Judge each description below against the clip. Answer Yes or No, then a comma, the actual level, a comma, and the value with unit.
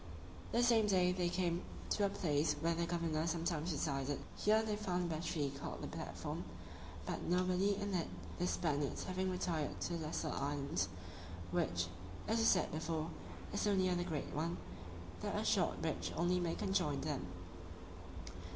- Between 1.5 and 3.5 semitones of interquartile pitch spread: Yes, average, 3.2 semitones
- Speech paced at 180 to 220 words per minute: No, average, 170 wpm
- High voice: No, medium, 170 Hz